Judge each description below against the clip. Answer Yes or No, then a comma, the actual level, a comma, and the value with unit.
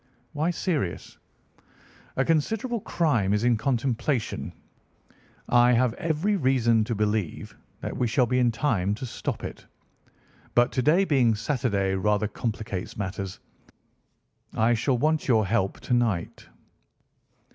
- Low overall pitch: Yes, low, 120 Hz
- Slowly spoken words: Yes, slow, 130 wpm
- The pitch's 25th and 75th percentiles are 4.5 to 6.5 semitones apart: Yes, average, 4.8 semitones